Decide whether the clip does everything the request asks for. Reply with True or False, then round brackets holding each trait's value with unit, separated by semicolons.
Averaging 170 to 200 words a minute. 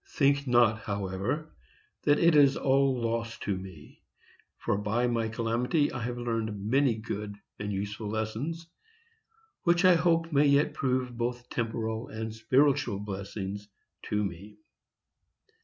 False (135 wpm)